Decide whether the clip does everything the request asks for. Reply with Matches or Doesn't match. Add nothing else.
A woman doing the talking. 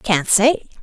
Matches